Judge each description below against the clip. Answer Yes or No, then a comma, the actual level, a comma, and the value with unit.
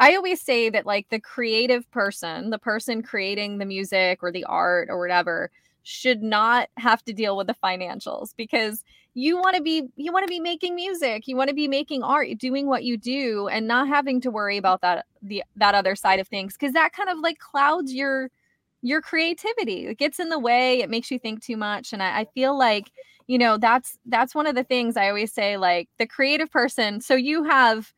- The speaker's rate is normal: No, fast, 220 wpm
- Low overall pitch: No, high, 245 Hz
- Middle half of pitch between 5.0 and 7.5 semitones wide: Yes, wide, 5.4 semitones